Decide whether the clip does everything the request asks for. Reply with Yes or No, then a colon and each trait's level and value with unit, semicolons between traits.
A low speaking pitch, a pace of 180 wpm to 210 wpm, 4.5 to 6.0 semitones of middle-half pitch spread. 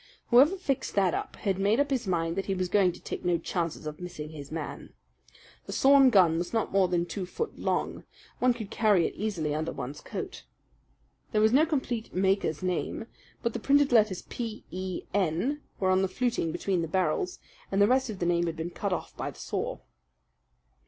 No: high, 195 Hz; fast, 205 wpm; average, 5.2 semitones